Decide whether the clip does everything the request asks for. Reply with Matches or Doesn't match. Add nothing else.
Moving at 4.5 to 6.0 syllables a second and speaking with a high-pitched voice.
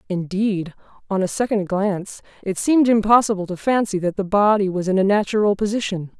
Matches